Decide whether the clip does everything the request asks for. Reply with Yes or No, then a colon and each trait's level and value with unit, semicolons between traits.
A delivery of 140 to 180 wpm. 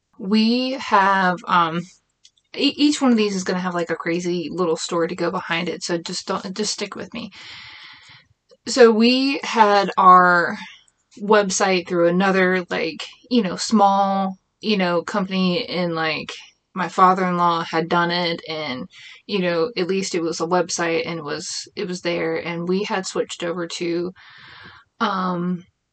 Yes: average, 165 wpm